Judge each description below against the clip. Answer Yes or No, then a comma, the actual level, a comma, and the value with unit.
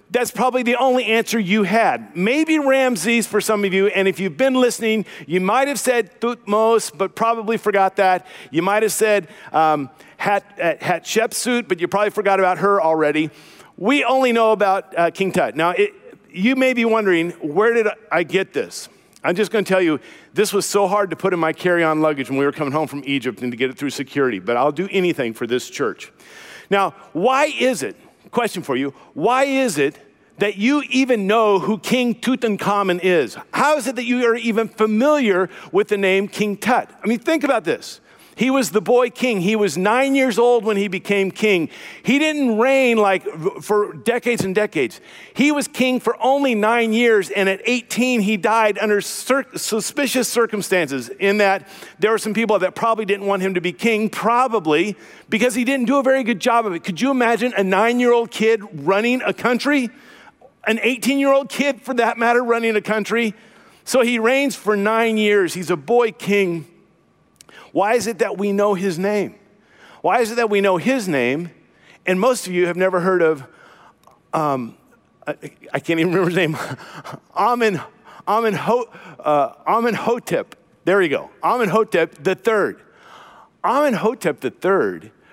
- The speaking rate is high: No, average, 185 wpm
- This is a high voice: Yes, high, 215 Hz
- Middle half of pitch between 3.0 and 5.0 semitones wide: Yes, average, 4.2 semitones